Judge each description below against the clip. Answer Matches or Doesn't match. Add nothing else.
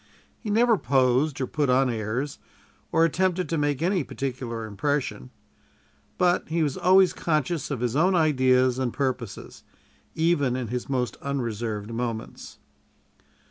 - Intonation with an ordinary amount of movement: Matches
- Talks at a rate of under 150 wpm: Matches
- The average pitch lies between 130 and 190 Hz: Matches